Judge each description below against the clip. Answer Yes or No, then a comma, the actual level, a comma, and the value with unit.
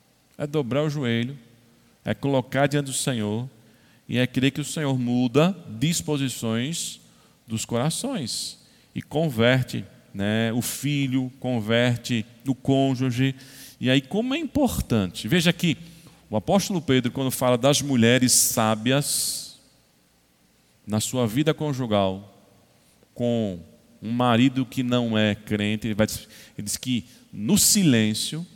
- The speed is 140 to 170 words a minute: No, average, 125 wpm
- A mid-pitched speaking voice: No, low, 125 Hz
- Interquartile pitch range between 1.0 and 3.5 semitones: No, average, 4.2 semitones